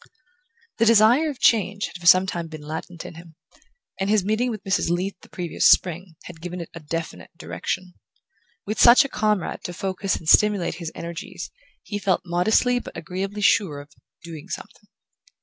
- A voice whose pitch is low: No, medium, 185 Hz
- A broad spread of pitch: No, average, 3.8 semitones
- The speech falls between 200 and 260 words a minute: No, average, 180 wpm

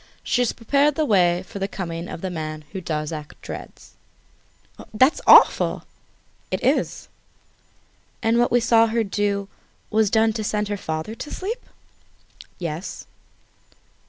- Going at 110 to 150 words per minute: Yes, average, 140 wpm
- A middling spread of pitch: Yes, average, 4.9 semitones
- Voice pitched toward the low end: No, high, 205 Hz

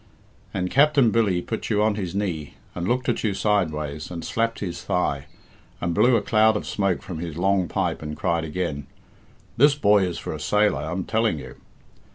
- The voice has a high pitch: No, very low, 95 Hz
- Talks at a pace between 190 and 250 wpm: Yes, average, 195 wpm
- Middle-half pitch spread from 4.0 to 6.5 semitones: Yes, average, 4.5 semitones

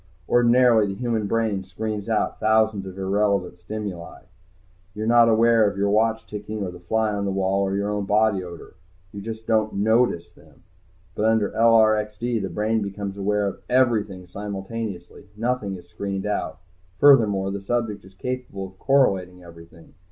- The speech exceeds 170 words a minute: No, average, 165 wpm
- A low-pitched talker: Yes, low, 105 Hz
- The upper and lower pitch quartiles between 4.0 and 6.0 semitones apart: No, narrow, 2.4 semitones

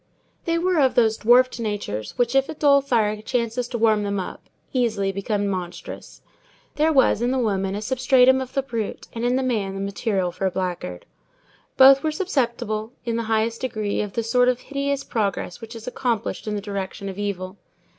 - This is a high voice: Yes, high, 230 Hz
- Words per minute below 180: No, average, 195 wpm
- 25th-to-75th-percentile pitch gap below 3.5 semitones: No, average, 4.2 semitones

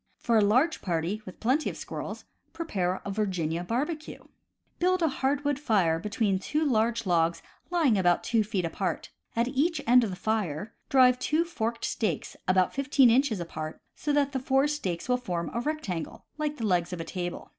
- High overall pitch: Yes, high, 225 Hz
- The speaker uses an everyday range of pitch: No, wide, 7.4 semitones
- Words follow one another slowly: No, average, 190 wpm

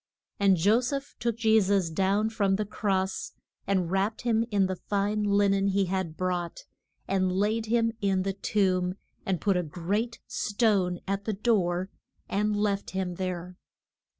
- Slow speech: No, average, 165 wpm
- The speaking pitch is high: Yes, high, 195 Hz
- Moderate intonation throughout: No, narrow, 2.2 semitones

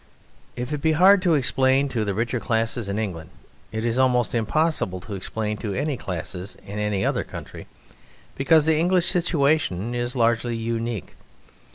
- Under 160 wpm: No, average, 165 wpm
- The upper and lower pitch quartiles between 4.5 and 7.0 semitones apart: Yes, wide, 5.4 semitones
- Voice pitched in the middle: No, low, 120 Hz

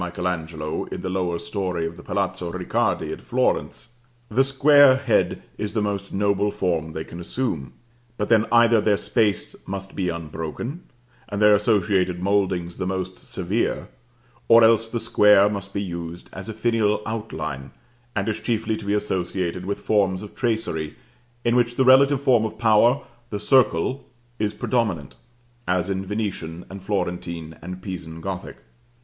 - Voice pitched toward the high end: No, low, 100 Hz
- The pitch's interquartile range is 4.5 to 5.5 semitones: No, average, 4.0 semitones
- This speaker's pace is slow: No, average, 160 wpm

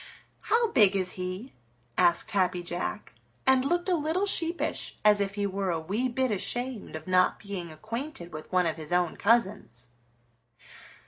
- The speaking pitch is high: Yes, high, 200 Hz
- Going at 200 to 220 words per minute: No, average, 165 wpm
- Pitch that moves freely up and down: Yes, wide, 6.2 semitones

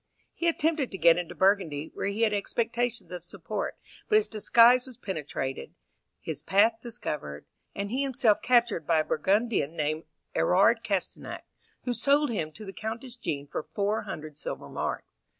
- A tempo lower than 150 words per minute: No, average, 165 wpm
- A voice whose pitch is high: Yes, high, 205 Hz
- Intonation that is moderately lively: No, wide, 6.1 semitones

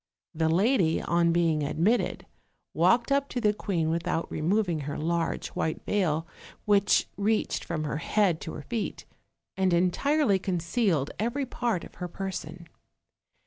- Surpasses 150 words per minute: No, average, 145 wpm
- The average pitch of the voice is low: No, medium, 180 Hz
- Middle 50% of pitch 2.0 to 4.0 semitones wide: No, average, 4.6 semitones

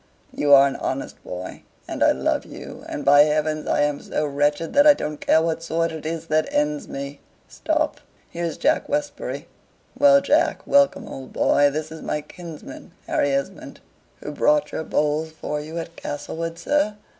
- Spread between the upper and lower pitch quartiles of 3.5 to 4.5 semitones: No, narrow, 2.6 semitones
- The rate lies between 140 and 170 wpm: No, average, 180 wpm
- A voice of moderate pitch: Yes, medium, 155 Hz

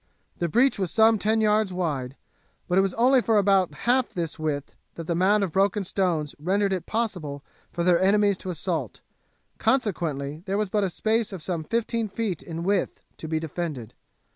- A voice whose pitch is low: No, high, 190 Hz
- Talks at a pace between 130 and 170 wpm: No, average, 190 wpm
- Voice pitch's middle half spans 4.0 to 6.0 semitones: Yes, average, 4.4 semitones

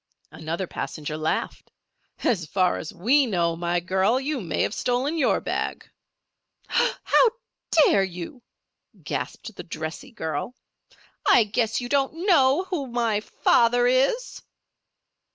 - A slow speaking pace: Yes, slow, 125 wpm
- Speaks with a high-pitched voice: Yes, high, 230 Hz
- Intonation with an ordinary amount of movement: No, wide, 7.4 semitones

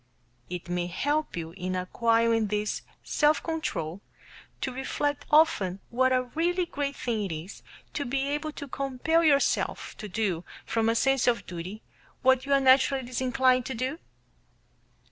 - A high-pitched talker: Yes, very high, 255 Hz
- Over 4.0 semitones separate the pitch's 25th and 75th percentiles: Yes, average, 5.2 semitones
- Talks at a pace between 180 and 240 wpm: No, average, 155 wpm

